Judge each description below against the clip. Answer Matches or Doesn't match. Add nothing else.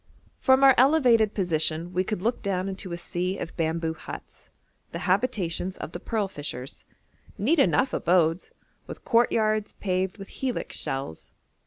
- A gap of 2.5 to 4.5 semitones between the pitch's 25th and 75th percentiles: Doesn't match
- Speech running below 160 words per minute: Matches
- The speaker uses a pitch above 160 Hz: Matches